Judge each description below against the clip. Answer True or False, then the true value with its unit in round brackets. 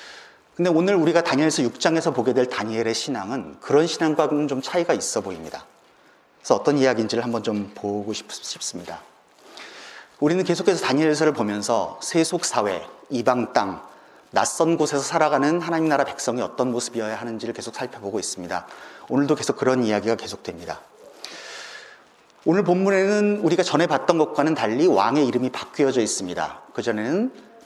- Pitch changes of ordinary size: False (5.8 semitones)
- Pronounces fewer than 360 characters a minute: False (370 characters per minute)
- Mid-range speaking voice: True (145 Hz)